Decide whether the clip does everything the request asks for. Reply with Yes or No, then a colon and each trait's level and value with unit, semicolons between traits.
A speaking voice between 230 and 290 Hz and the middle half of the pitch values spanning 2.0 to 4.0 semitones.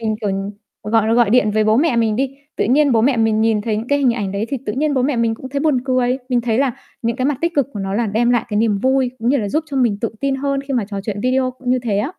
Yes: high, 240 Hz; average, 3.5 semitones